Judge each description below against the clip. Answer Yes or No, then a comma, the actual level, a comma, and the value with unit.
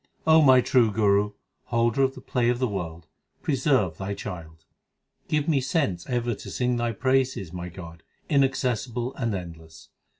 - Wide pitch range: Yes, wide, 5.9 semitones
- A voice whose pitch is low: Yes, low, 120 Hz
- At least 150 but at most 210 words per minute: Yes, average, 165 wpm